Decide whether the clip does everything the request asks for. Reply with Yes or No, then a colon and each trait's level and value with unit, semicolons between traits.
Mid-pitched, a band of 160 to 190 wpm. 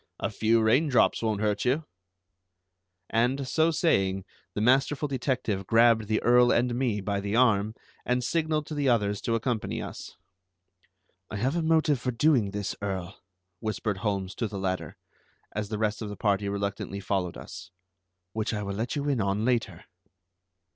No: low, 110 Hz; average, 170 wpm